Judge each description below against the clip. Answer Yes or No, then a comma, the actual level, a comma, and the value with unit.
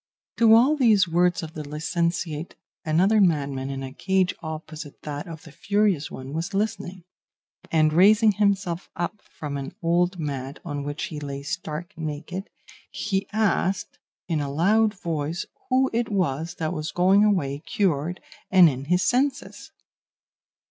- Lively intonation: No, average, 4.6 semitones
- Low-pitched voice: No, medium, 170 Hz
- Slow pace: No, average, 150 wpm